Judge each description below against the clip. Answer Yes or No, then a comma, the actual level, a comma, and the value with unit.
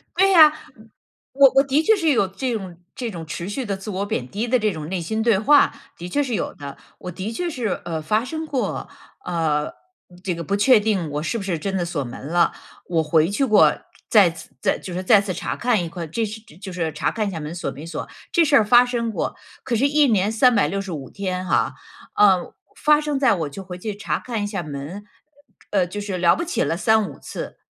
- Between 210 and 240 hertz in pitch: No, high, 200 Hz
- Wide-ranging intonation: Yes, wide, 5.7 semitones